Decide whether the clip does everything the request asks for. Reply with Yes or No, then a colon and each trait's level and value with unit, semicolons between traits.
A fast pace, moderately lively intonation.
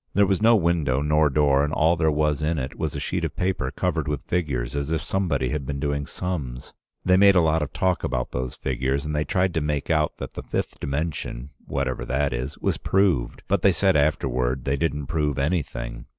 Yes: fast, 220 wpm; average, 3.4 semitones